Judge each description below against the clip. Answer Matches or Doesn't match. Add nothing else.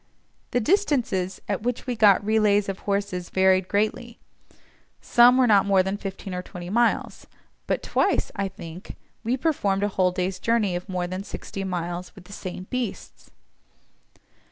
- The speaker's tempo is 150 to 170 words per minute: Matches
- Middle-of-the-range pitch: Doesn't match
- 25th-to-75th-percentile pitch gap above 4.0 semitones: Doesn't match